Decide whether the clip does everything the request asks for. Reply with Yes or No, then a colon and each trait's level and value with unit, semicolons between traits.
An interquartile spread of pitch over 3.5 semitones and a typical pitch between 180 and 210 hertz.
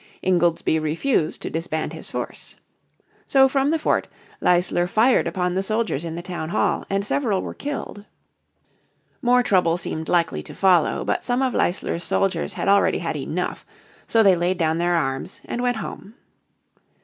Yes: average, 5.2 semitones; medium, 185 Hz